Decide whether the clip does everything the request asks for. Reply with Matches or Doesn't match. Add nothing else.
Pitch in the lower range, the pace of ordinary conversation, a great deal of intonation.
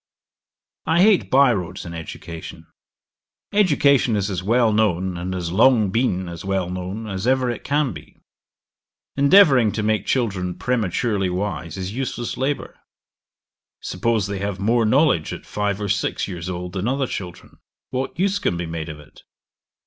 Matches